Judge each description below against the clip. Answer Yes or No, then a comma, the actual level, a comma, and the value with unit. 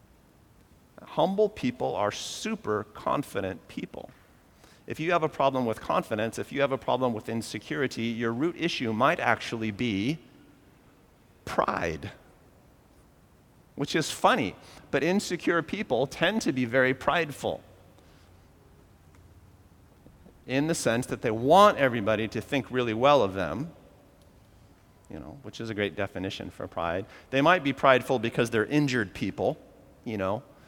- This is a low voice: Yes, low, 115 Hz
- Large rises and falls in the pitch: Yes, wide, 5.7 semitones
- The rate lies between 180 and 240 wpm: No, slow, 135 wpm